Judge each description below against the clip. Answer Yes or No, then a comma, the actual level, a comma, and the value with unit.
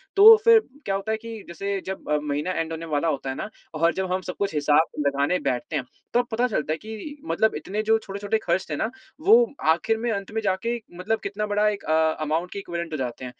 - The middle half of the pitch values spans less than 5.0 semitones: No, wide, 5.6 semitones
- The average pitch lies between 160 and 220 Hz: Yes, high, 190 Hz